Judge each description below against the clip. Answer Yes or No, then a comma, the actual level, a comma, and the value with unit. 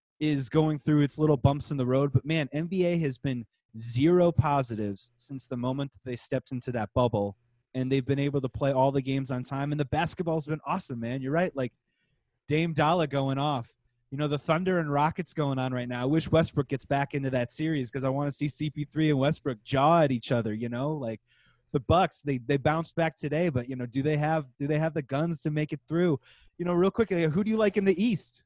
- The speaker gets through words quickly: Yes, fast, 245 wpm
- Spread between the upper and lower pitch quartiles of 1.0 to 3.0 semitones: No, average, 3.4 semitones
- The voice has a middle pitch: Yes, medium, 145 Hz